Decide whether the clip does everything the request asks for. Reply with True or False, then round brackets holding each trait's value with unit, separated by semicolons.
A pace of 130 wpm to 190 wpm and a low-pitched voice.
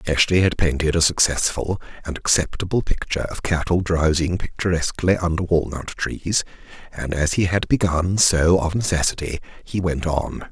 True (150 wpm; 85 Hz)